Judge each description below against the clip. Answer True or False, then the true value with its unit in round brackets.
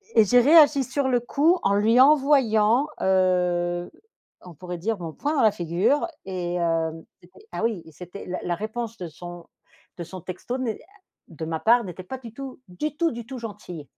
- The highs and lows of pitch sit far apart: True (6.6 semitones)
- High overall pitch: True (210 Hz)